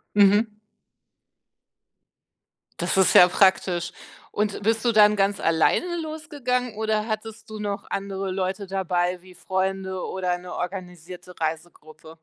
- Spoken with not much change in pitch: No, average, 3.0 semitones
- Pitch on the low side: No, high, 195 Hz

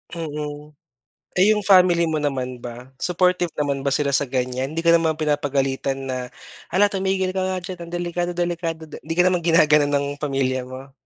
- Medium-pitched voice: Yes, medium, 150 Hz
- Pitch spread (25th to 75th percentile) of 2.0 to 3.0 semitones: No, average, 4.4 semitones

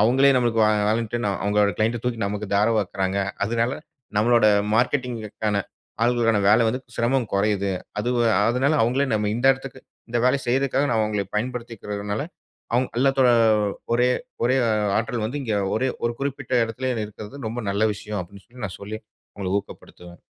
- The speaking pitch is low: Yes, low, 115 Hz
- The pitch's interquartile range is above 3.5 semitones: No, average, 3.2 semitones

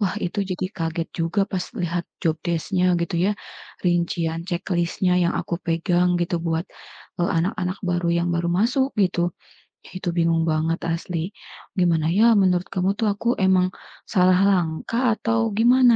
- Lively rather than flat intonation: No, narrow, 2.4 semitones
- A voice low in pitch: No, medium, 180 Hz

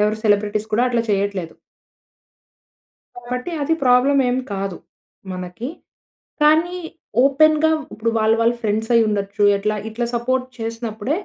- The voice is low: No, high, 230 Hz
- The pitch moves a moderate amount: Yes, average, 3.5 semitones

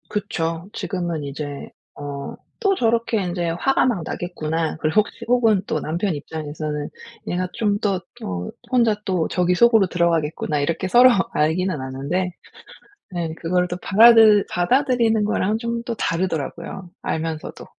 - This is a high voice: No, medium, 180 Hz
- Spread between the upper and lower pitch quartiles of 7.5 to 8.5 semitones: No, average, 5.3 semitones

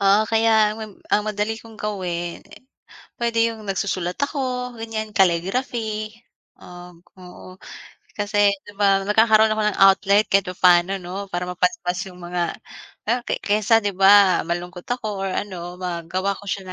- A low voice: No, high, 200 Hz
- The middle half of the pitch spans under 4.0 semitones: Yes, average, 3.2 semitones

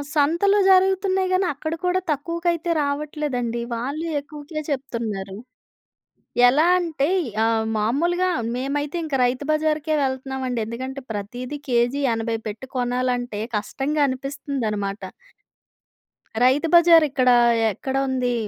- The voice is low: No, very high, 275 Hz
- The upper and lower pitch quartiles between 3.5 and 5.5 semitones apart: Yes, average, 4.0 semitones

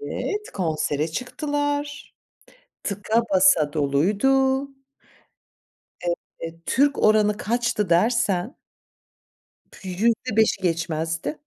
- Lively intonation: Yes, wide, 8.0 semitones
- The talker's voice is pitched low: No, high, 210 Hz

